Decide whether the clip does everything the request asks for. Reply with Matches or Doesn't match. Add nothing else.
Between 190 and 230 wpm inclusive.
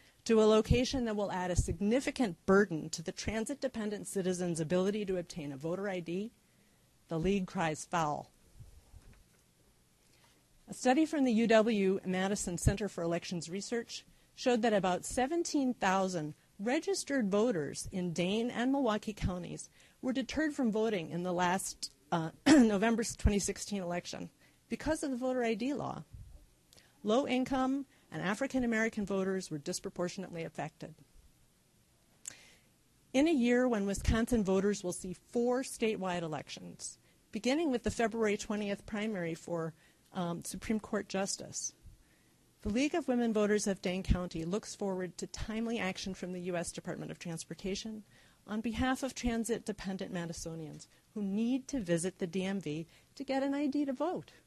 Doesn't match